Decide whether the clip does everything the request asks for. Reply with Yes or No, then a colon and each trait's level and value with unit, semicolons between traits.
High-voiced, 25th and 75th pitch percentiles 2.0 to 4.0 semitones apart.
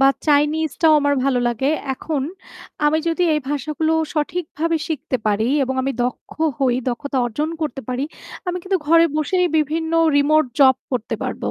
Yes: very high, 295 Hz; average, 3.2 semitones